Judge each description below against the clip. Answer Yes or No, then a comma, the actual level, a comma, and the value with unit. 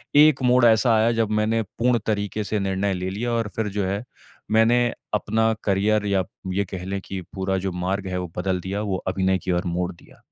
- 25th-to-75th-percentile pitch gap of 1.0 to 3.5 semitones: Yes, average, 3.0 semitones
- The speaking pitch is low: Yes, low, 100 Hz